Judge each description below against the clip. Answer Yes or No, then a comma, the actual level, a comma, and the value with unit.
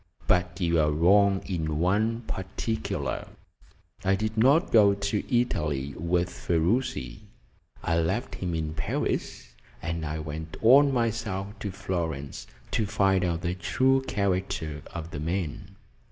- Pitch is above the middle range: No, very low, 90 Hz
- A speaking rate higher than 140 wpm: No, slow, 135 wpm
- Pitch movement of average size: Yes, average, 4.2 semitones